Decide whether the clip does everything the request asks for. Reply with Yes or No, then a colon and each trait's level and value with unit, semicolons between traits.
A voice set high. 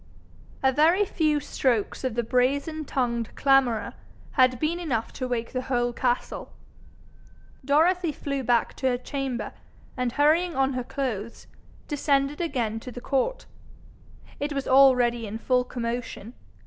Yes: very high, 260 Hz